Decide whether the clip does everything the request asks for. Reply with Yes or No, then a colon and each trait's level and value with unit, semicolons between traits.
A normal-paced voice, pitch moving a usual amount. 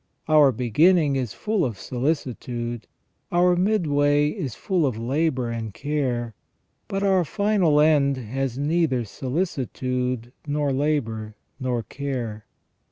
No: slow, 115 wpm; average, 4.4 semitones